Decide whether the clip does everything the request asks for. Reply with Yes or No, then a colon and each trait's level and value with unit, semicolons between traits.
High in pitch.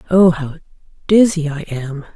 No: medium, 160 Hz